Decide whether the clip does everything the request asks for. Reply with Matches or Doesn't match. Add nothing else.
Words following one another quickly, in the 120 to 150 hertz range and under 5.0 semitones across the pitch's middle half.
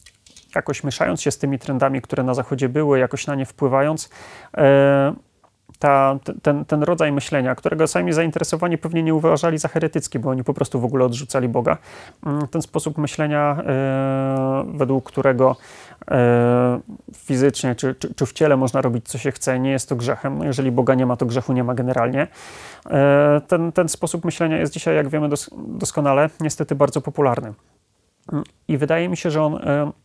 Matches